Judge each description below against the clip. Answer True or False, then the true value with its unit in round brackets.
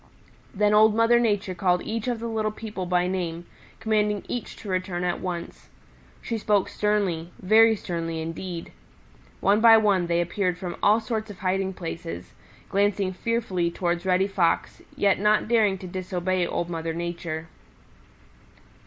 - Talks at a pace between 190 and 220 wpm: False (155 wpm)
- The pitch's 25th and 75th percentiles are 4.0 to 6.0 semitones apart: False (3.3 semitones)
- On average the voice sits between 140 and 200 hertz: True (190 Hz)